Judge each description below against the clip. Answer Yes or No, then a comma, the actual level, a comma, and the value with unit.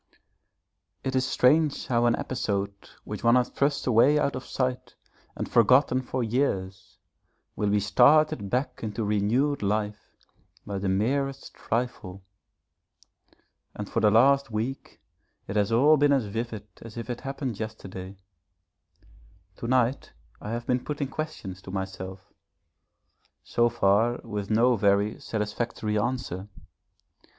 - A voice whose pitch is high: No, low, 115 Hz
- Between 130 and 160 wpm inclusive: Yes, slow, 135 wpm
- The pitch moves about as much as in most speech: Yes, average, 3.9 semitones